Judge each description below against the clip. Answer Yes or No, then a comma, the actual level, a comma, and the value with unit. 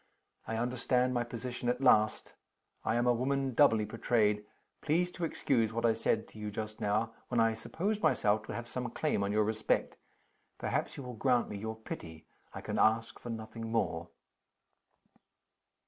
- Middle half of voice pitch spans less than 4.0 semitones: Yes, narrow, 2.4 semitones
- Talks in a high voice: No, low, 115 Hz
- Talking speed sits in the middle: Yes, average, 175 wpm